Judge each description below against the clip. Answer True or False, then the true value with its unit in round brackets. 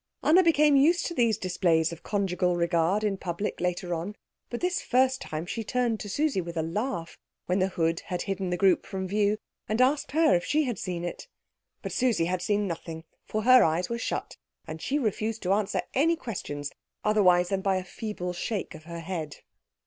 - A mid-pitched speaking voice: False (195 Hz)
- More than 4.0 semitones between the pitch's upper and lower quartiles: True (5.2 semitones)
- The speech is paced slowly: False (200 wpm)